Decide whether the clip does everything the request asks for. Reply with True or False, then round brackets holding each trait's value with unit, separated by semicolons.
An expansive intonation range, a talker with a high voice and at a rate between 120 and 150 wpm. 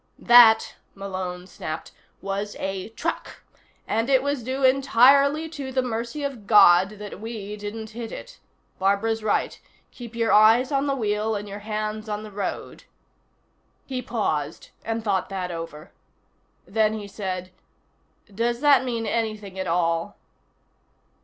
False (3.4 semitones; 215 Hz; 140 wpm)